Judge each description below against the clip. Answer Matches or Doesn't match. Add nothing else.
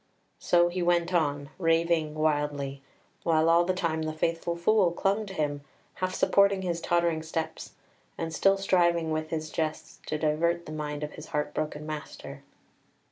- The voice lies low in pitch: Doesn't match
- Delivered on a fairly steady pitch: Matches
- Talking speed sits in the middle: Matches